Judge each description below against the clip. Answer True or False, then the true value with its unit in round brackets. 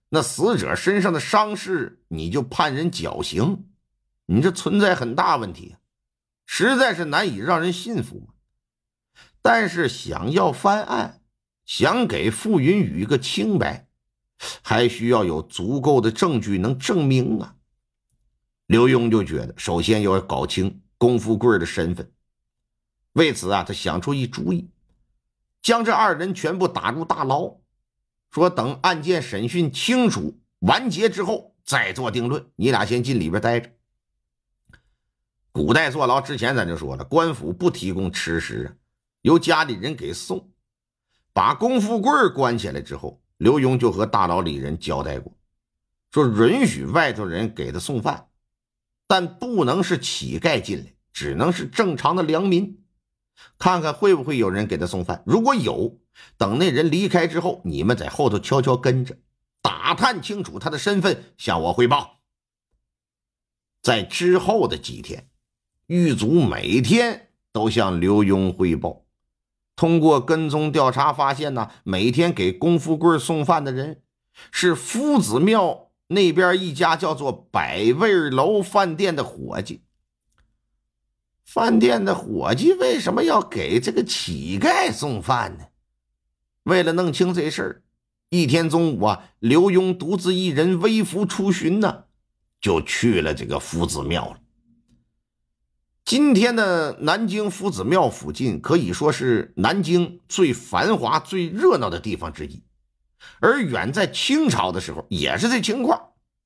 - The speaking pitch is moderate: True (155 Hz)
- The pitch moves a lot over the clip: True (8.6 semitones)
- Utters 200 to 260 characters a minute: True (210 characters per minute)